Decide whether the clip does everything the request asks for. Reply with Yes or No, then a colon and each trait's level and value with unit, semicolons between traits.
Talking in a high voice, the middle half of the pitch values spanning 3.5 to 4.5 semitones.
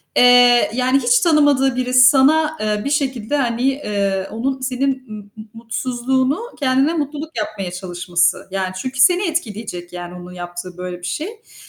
No: high, 245 Hz; wide, 5.5 semitones